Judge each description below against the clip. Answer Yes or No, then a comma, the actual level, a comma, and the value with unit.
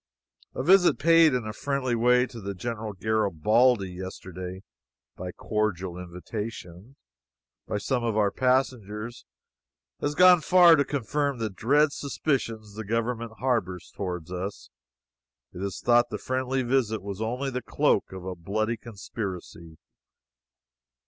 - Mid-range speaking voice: No, low, 110 Hz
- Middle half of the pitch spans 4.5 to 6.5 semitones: Yes, average, 5.1 semitones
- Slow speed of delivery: Yes, slow, 130 wpm